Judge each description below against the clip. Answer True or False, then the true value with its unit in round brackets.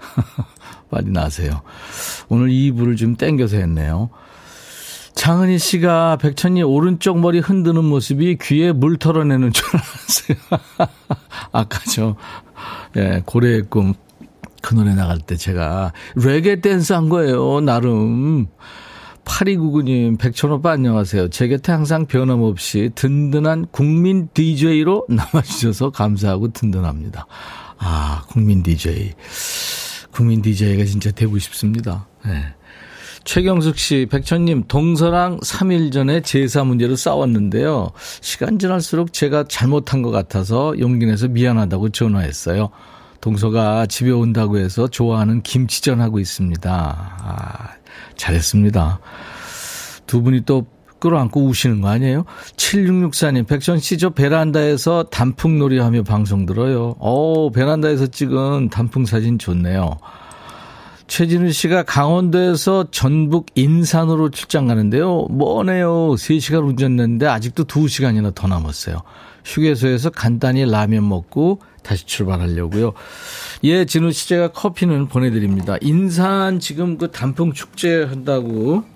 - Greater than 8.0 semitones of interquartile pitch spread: False (7.1 semitones)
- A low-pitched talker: True (130 Hz)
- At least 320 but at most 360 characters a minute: False (275 characters per minute)